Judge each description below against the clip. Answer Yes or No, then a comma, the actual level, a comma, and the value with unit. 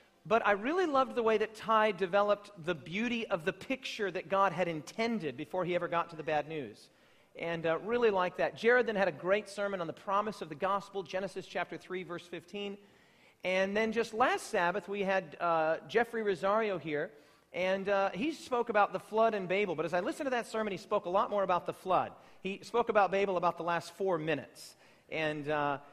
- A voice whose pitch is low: No, high, 195 Hz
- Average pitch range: Yes, average, 3.9 semitones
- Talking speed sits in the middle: No, fast, 220 wpm